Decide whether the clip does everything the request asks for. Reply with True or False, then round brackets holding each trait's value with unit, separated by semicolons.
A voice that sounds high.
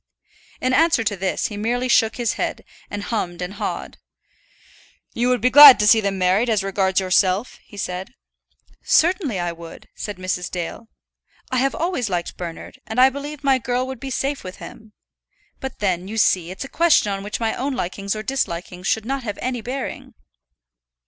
True (220 Hz)